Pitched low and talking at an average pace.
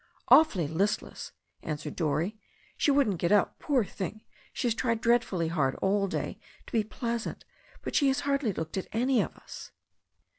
No: high, 210 Hz; average, 170 wpm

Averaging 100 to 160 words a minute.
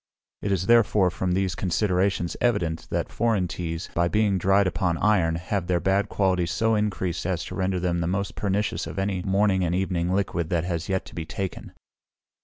No: average, 190 wpm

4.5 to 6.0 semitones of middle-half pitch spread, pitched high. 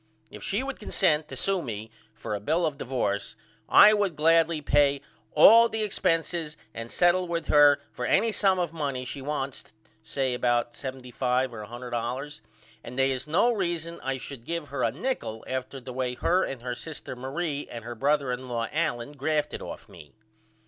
No: average, 5.1 semitones; medium, 140 Hz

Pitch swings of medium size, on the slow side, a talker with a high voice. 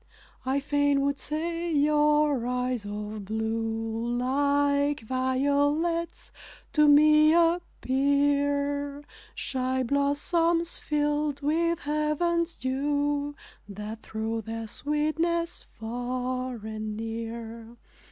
Yes: average, 4.1 semitones; slow, 85 wpm; very high, 280 Hz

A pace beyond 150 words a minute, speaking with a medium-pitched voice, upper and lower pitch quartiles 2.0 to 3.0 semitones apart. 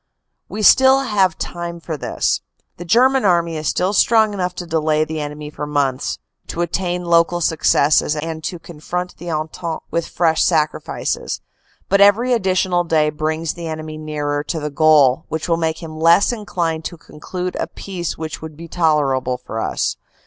Yes: average, 175 wpm; medium, 165 Hz; narrow, 2.6 semitones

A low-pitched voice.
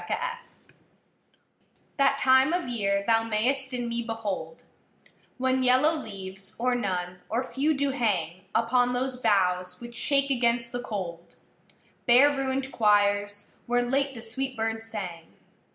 No: high, 235 Hz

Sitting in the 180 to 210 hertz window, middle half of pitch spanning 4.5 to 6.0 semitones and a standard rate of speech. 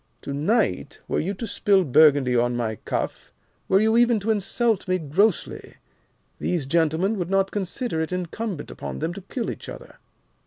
Yes: medium, 185 Hz; wide, 5.4 semitones; average, 170 wpm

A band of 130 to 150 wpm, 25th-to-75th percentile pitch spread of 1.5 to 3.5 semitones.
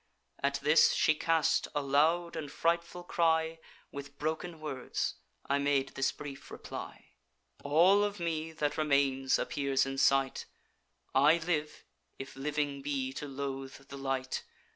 Yes: average, 140 wpm; average, 2.9 semitones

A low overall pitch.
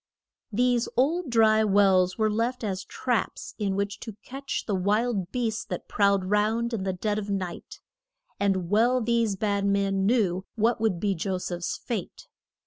No: high, 210 Hz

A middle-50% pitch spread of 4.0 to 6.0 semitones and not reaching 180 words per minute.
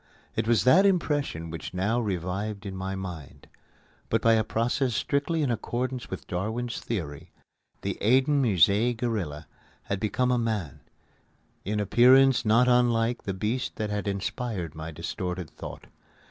Yes: average, 4.6 semitones; average, 145 wpm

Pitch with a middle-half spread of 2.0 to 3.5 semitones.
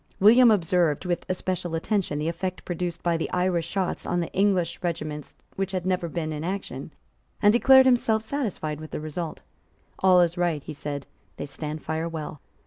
Yes: average, 3.1 semitones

